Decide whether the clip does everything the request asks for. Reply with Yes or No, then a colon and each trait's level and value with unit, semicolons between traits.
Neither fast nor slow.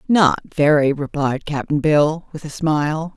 Yes: average, 150 wpm